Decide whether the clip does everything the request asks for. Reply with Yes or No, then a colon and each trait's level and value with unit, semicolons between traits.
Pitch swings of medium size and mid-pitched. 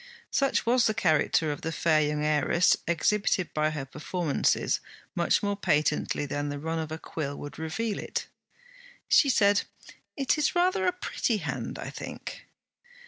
No: wide, 6.2 semitones; medium, 165 Hz